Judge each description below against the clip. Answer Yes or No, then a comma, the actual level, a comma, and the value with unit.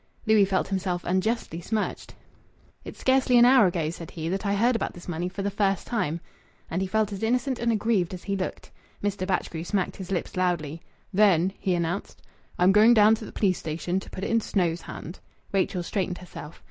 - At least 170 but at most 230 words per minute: Yes, fast, 205 wpm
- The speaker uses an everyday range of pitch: Yes, average, 3.4 semitones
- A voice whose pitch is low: No, high, 190 Hz